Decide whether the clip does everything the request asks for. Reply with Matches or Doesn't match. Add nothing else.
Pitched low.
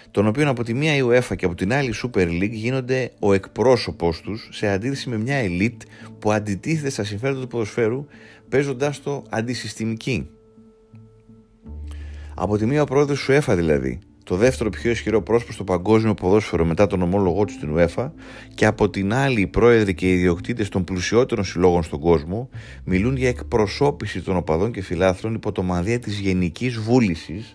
Matches